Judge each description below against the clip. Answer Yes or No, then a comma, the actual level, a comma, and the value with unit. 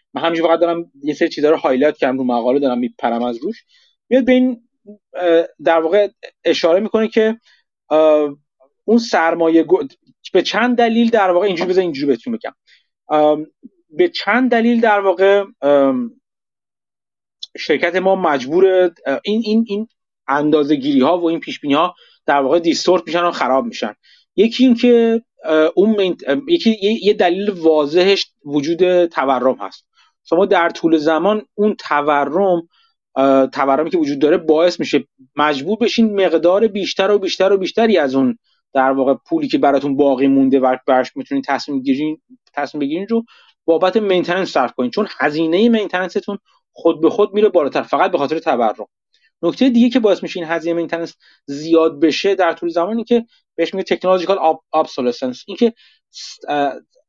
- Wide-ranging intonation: Yes, wide, 6.1 semitones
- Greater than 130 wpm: Yes, average, 150 wpm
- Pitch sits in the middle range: Yes, medium, 175 Hz